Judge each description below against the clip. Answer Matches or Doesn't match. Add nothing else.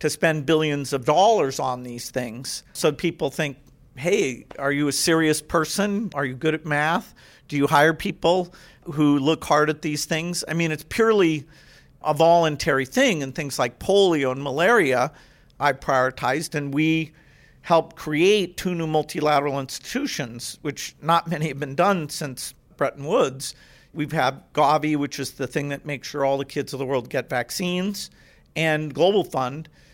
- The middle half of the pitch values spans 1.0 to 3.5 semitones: Matches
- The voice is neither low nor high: Matches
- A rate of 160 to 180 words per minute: Matches